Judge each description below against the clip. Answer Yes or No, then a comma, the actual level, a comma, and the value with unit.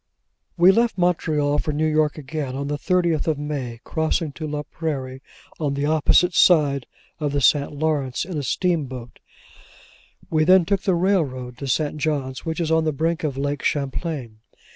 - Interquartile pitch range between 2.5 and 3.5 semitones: Yes, average, 2.8 semitones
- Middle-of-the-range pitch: Yes, medium, 150 Hz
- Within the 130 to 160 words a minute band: No, average, 175 wpm